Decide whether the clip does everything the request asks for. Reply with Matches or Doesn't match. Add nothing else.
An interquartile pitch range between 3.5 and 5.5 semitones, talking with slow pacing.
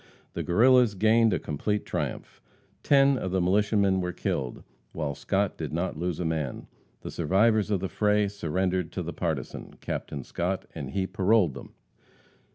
Doesn't match